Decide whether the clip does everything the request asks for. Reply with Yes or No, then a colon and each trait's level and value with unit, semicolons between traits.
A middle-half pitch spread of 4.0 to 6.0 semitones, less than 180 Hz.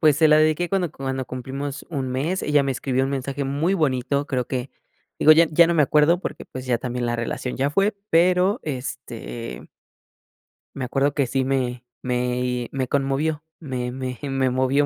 No: average, 3.1 semitones; low, 135 Hz